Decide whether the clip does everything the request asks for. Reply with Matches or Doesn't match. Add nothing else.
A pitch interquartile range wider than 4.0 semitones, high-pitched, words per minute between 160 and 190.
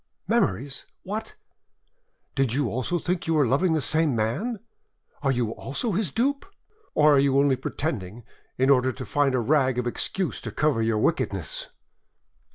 Doesn't match